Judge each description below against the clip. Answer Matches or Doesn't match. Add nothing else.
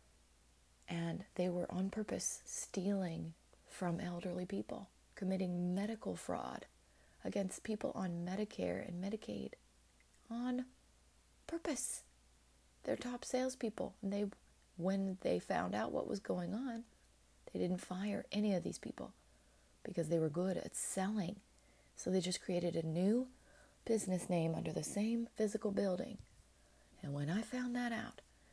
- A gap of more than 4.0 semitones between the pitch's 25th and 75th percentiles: Matches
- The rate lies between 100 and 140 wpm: Matches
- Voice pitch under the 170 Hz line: Doesn't match